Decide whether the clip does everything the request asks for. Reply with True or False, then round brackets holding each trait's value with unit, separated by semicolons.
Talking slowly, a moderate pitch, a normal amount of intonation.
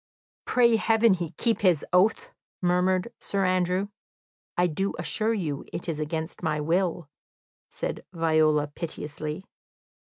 True (125 wpm; 180 Hz; 3.8 semitones)